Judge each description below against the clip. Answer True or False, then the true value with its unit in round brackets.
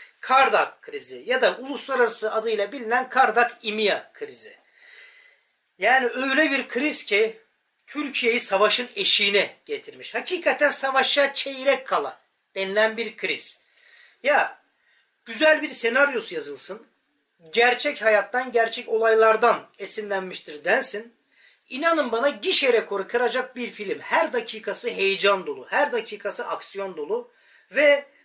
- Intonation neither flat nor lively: False (8.7 semitones)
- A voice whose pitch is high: True (260 Hz)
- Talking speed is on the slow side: False (115 wpm)